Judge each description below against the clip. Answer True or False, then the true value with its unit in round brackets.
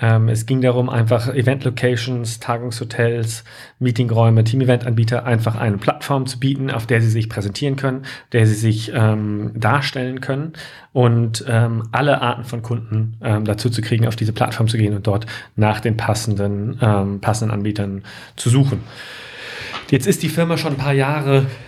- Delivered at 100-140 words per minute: False (160 wpm)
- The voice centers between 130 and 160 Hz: False (120 Hz)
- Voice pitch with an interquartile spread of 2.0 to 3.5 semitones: True (2.7 semitones)